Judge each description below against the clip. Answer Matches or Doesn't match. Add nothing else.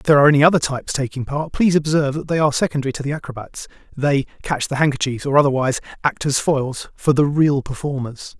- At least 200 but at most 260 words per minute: Matches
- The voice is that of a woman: Doesn't match